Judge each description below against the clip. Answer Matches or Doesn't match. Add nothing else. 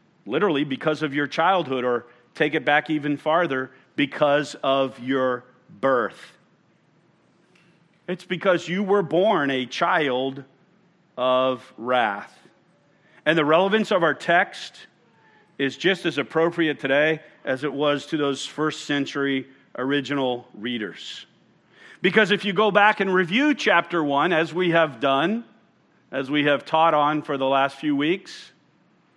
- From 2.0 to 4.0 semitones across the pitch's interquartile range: Doesn't match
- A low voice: Doesn't match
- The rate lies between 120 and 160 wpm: Matches